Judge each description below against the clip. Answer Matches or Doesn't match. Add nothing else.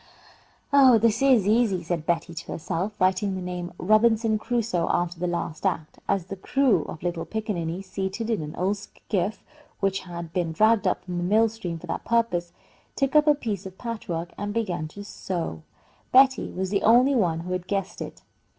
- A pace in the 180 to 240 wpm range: Matches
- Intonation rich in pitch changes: Doesn't match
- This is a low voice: Doesn't match